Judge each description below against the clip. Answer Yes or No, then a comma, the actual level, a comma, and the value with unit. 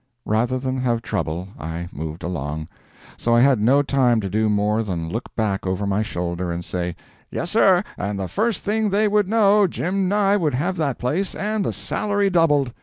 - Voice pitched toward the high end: No, low, 125 Hz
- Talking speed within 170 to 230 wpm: Yes, average, 195 wpm